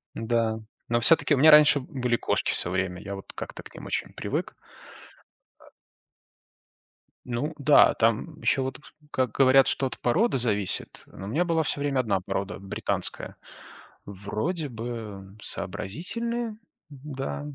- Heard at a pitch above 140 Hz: No, low, 125 Hz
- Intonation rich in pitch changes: Yes, wide, 6.3 semitones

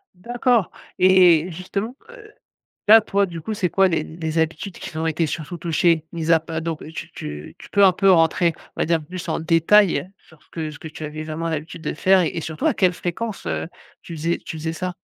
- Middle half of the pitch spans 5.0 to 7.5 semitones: No, average, 2.8 semitones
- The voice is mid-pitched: Yes, medium, 170 Hz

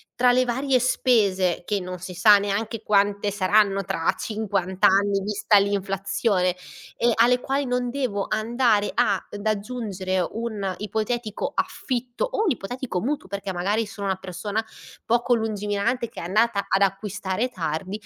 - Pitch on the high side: Yes, high, 205 Hz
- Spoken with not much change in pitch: No, average, 3.3 semitones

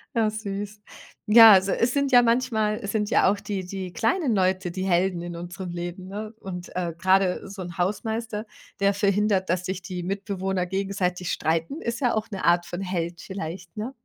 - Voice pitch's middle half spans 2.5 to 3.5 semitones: Yes, average, 2.9 semitones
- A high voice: Yes, high, 195 Hz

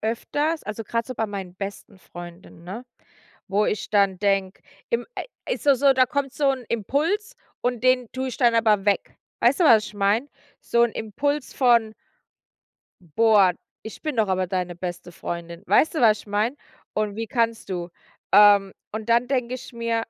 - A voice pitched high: Yes, high, 220 Hz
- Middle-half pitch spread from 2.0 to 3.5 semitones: No, average, 4.2 semitones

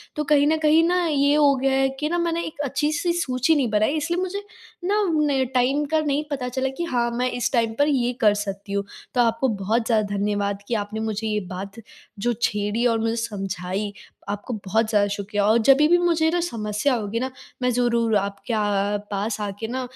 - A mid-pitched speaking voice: No, high, 240 Hz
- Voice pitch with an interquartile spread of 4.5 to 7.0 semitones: Yes, wide, 5.6 semitones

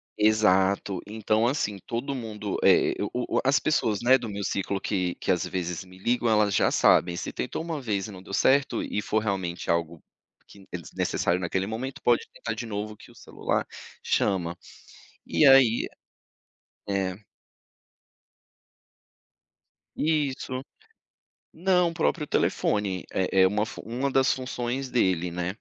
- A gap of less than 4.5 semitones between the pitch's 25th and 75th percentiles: No, average, 5.2 semitones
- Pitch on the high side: No, low, 105 Hz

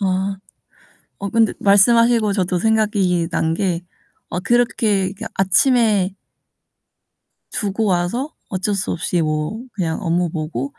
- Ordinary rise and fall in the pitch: Yes, average, 3.7 semitones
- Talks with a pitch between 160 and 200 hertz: Yes, high, 195 Hz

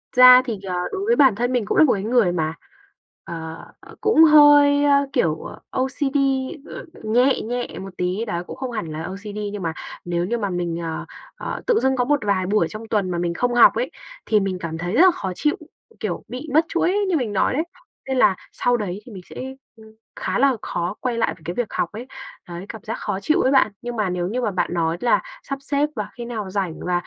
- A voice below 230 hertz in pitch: Yes, high, 220 Hz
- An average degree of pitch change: No, wide, 6.4 semitones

